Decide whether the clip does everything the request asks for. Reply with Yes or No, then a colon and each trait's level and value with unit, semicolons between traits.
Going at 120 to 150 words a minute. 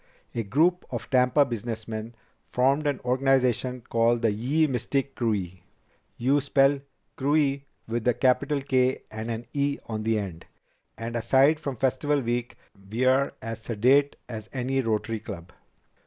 Yes: average, 140 wpm